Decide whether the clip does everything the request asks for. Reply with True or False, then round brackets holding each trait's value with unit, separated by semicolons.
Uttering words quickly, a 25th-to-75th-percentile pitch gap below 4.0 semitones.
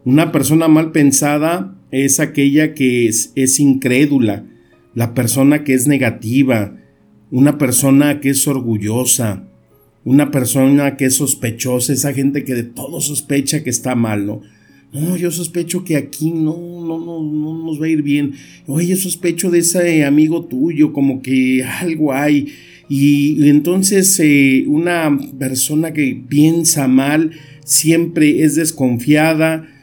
False (145 wpm; 3.1 semitones)